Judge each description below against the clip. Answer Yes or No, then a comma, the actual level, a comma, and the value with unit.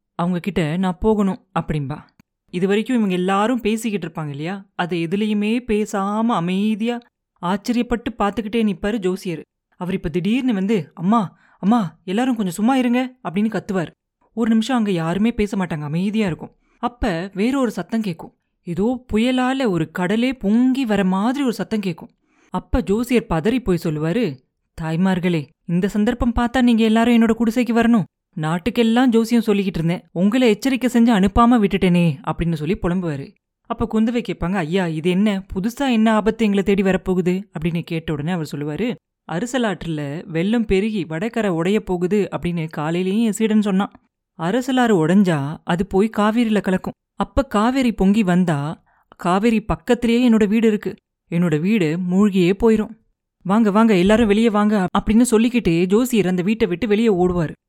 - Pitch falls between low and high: No, high, 205 Hz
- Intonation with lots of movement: No, average, 4.3 semitones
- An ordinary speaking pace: No, fast, 145 wpm